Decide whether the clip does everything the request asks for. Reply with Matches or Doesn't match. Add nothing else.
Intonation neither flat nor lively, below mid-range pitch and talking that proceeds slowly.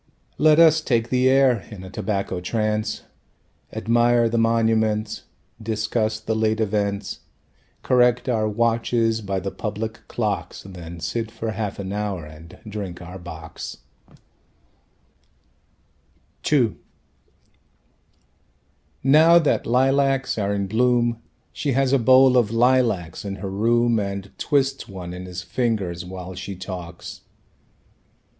Matches